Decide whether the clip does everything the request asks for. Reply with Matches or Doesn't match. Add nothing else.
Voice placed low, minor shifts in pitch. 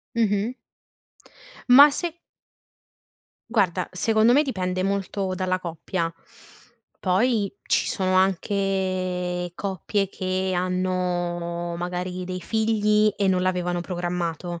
Doesn't match